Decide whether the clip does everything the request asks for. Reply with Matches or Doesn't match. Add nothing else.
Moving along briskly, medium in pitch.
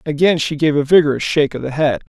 Matches